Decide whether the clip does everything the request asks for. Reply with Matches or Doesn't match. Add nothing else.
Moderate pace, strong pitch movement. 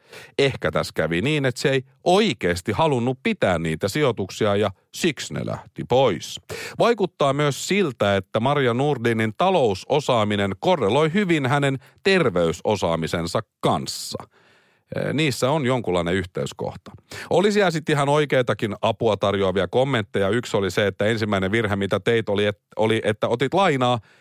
Matches